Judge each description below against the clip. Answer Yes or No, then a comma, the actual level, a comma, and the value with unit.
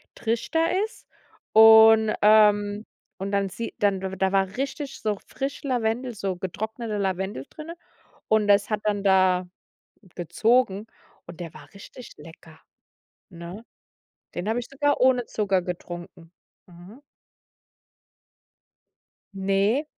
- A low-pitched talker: No, high, 205 Hz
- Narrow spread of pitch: No, average, 3.2 semitones